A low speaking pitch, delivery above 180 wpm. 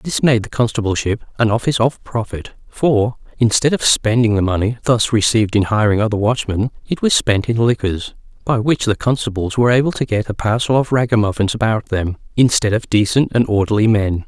Yes: low, 110 Hz; average, 190 wpm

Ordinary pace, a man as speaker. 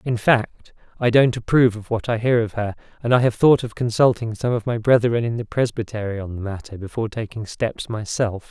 No: fast, 220 wpm; male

